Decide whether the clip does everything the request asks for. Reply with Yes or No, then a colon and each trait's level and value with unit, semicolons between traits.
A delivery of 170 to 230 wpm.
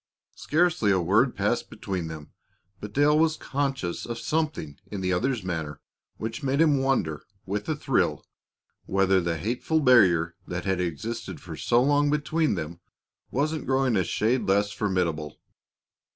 No: average, 150 wpm